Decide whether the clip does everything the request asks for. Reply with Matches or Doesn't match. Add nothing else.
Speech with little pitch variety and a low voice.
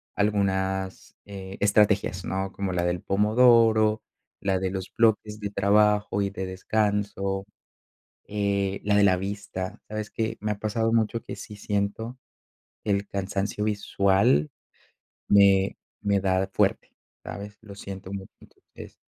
Matches